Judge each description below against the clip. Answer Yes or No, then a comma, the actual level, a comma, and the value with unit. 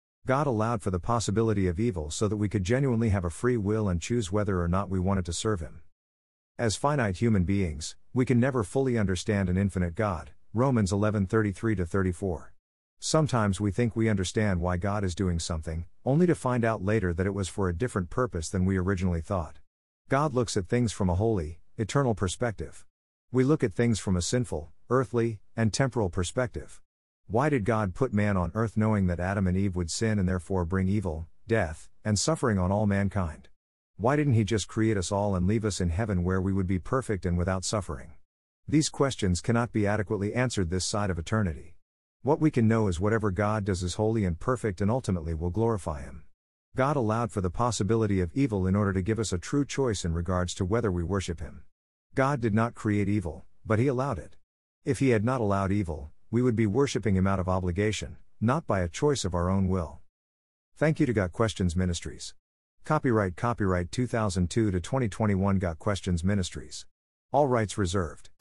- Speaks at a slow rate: No, average, 200 wpm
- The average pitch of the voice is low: Yes, low, 100 Hz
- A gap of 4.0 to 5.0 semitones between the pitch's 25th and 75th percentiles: Yes, average, 4.3 semitones